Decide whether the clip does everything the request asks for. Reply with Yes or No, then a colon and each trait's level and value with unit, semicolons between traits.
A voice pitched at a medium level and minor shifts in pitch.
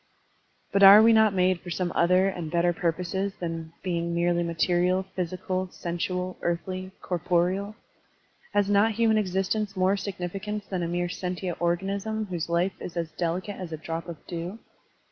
Yes: medium, 180 Hz; narrow, 2.2 semitones